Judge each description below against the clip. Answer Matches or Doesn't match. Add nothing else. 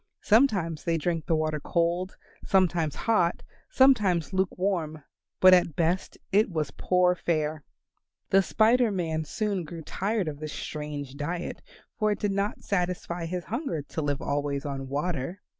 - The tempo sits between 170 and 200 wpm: Doesn't match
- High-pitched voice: Doesn't match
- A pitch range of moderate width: Matches